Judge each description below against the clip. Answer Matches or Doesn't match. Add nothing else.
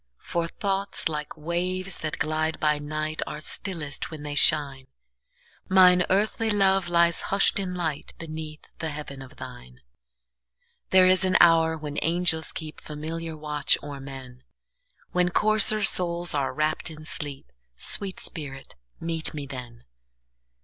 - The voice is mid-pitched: Matches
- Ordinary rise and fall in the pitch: Matches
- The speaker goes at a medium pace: Doesn't match